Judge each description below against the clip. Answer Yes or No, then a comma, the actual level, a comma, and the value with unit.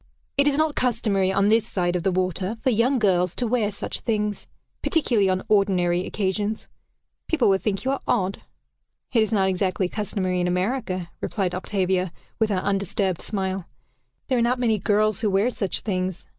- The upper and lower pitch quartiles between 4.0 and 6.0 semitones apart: No, average, 3.2 semitones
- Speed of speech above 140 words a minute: Yes, average, 180 wpm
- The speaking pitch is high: Yes, high, 200 Hz